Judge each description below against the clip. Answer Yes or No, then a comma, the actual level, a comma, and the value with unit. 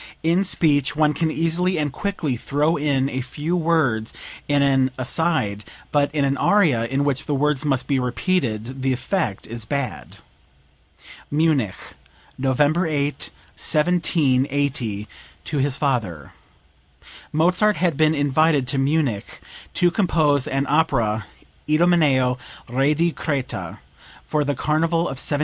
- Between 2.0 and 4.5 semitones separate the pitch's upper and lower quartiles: Yes, average, 3.5 semitones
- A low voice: No, medium, 145 Hz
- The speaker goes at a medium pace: No, slow, 130 wpm